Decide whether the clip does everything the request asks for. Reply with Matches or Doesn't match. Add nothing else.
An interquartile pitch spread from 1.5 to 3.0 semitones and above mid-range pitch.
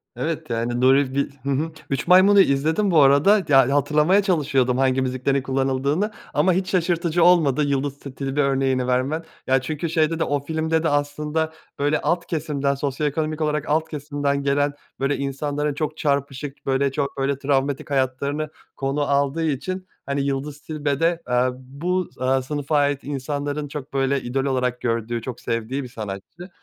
Doesn't match